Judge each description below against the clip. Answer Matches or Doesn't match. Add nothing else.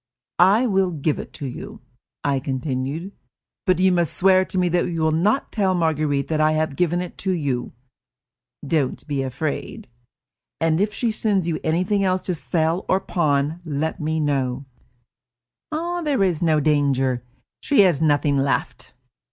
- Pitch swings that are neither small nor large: Matches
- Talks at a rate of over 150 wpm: Matches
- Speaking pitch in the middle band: Matches